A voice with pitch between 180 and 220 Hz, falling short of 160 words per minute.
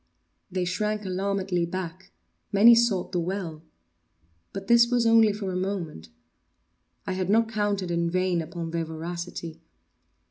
Yes: medium, 185 Hz; average, 140 wpm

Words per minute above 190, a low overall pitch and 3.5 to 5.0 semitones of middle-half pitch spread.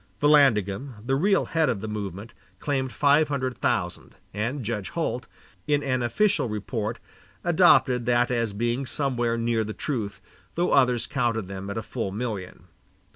No: average, 155 wpm; low, 120 Hz; average, 4.3 semitones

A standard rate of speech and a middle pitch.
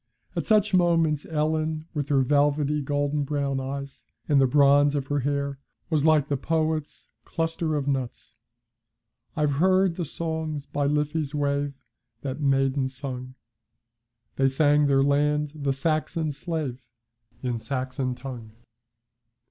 No: slow, 130 wpm; medium, 145 Hz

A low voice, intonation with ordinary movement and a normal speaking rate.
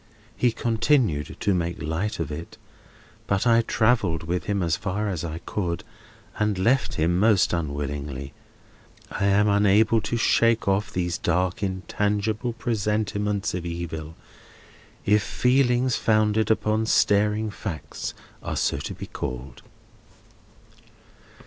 No: low, 100 Hz; average, 4.3 semitones; slow, 125 wpm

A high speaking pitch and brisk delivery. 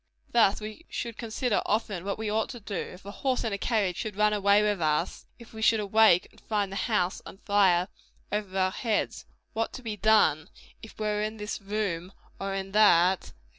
Yes: high, 210 Hz; fast, 210 wpm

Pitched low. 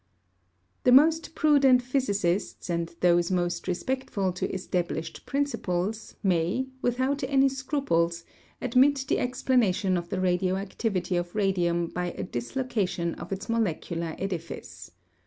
No: high, 190 Hz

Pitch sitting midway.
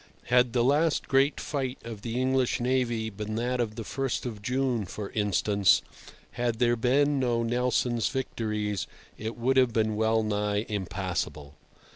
No: low, 115 Hz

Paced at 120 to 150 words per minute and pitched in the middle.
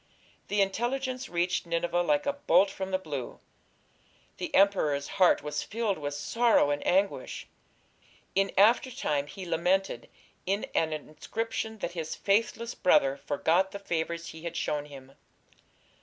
Yes: average, 140 wpm; medium, 180 Hz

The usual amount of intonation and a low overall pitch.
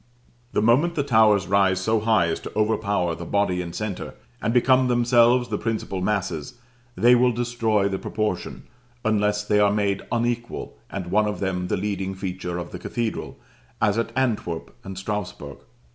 Yes: average, 3.4 semitones; low, 105 Hz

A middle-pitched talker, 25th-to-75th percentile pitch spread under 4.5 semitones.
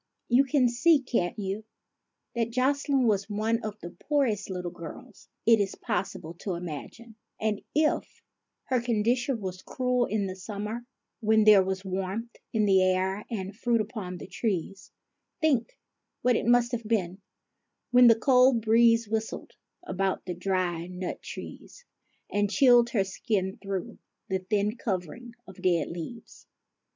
No: high, 215 Hz; average, 4.0 semitones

